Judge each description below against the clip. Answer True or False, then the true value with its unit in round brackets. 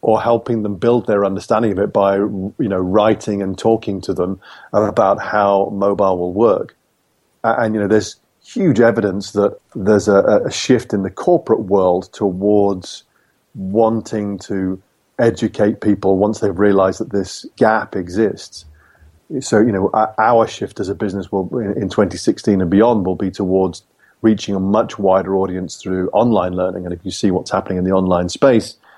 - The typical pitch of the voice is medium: False (100 Hz)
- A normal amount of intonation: False (2.2 semitones)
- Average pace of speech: True (170 wpm)